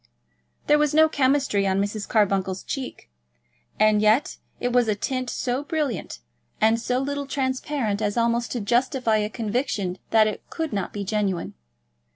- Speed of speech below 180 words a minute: Yes, average, 160 wpm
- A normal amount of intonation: Yes, average, 4.3 semitones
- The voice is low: No, high, 230 Hz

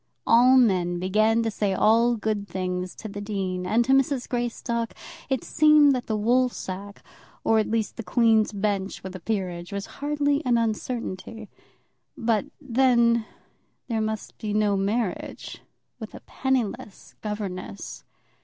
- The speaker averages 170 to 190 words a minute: No, average, 145 wpm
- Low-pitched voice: No, high, 220 Hz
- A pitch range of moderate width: Yes, average, 3.2 semitones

